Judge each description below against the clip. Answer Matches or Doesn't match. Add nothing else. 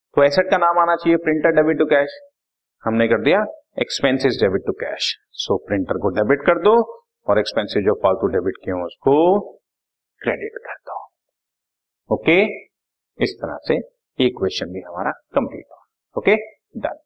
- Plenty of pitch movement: Matches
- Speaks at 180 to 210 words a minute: Doesn't match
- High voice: Doesn't match